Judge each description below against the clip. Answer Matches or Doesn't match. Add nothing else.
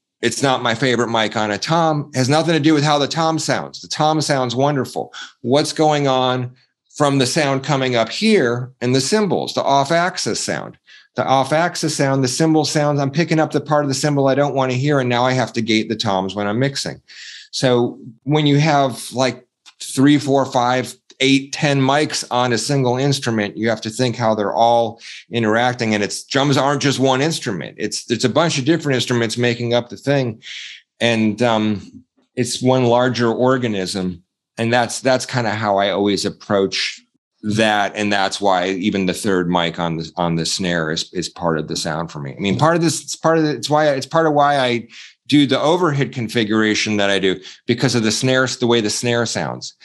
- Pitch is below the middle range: Matches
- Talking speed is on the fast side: Matches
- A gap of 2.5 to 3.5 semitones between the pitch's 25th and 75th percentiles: Doesn't match